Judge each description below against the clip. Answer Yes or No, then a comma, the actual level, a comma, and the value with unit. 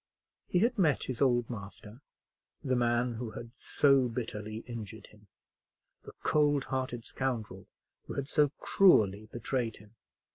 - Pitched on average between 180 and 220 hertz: No, low, 120 Hz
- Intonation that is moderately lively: Yes, average, 3.6 semitones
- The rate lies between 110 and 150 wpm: Yes, average, 140 wpm